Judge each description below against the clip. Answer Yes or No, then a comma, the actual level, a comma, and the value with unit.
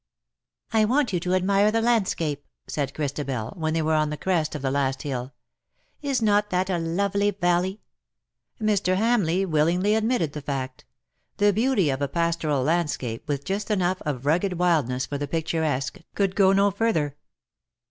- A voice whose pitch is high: No, medium, 170 Hz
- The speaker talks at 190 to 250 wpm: No, average, 180 wpm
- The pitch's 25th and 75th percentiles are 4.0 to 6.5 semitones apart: Yes, wide, 5.5 semitones